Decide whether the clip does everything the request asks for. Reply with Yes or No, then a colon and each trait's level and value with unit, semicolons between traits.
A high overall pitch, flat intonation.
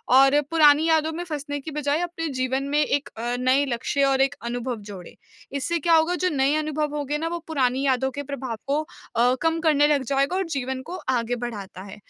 No: very high, 280 Hz; average, 3.1 semitones